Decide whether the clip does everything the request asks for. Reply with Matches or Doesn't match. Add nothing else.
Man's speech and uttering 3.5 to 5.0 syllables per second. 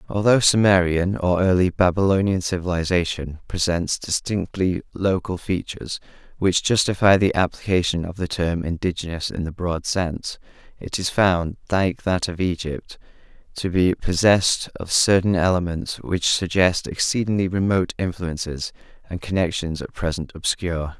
Matches